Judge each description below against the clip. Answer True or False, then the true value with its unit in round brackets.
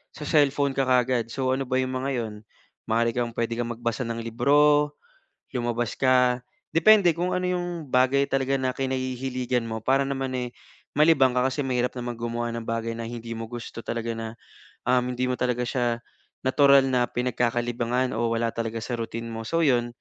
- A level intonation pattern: True (2.3 semitones)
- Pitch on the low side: True (125 Hz)